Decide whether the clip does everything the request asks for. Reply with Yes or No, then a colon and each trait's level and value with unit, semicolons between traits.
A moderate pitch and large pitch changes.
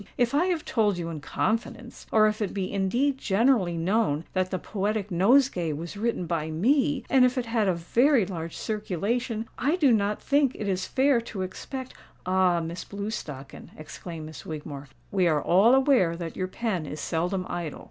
No: high, 200 Hz; wide, 5.8 semitones